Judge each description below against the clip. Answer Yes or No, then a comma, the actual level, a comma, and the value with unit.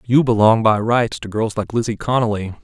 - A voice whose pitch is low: Yes, low, 110 Hz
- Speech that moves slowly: No, fast, 205 wpm